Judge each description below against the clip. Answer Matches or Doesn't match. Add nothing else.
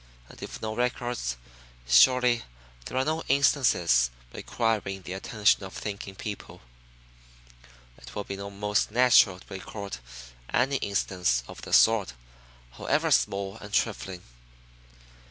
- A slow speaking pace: Matches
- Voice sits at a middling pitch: Doesn't match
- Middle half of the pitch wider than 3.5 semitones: Matches